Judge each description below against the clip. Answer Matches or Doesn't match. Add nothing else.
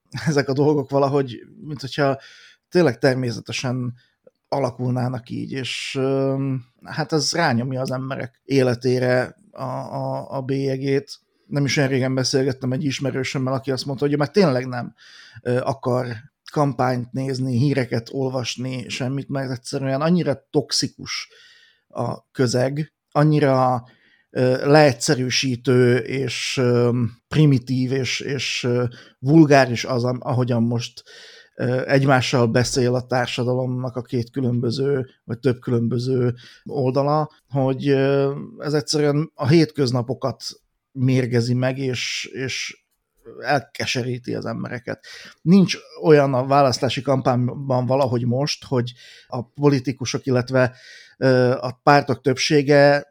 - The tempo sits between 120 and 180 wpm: Doesn't match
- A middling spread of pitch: Doesn't match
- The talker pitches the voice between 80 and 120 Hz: Doesn't match